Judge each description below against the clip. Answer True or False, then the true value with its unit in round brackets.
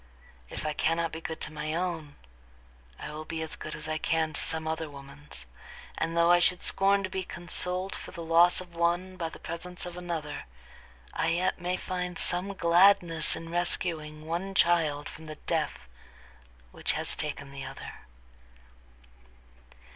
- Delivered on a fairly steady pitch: True (2.3 semitones)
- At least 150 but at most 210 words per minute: True (170 wpm)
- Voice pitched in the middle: True (165 Hz)